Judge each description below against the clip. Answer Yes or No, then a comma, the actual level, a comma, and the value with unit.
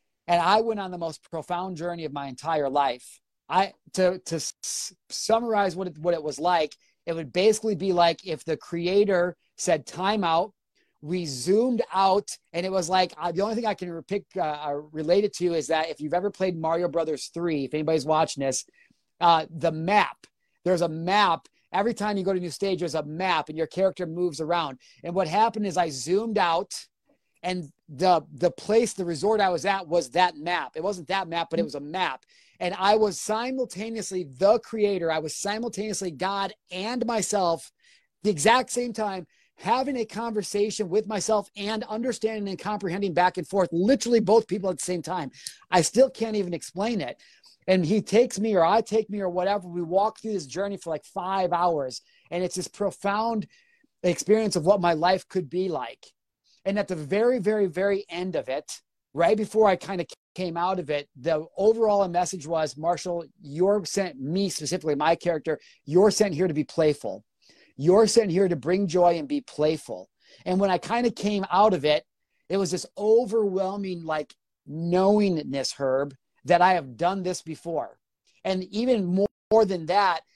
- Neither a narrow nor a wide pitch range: Yes, average, 3.6 semitones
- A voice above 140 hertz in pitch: Yes, medium, 185 Hz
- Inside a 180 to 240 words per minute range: Yes, average, 195 wpm